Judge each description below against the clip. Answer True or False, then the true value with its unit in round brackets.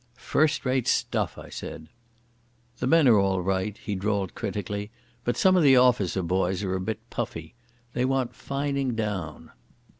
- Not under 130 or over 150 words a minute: False (160 wpm)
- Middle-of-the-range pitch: False (105 Hz)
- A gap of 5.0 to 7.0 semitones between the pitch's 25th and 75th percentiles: True (5.4 semitones)